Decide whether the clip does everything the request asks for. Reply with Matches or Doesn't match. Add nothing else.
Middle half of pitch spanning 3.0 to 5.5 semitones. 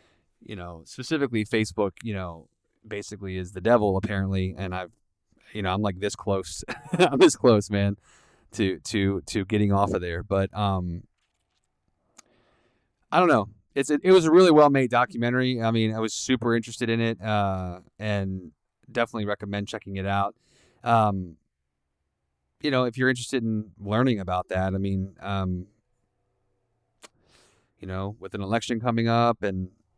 Matches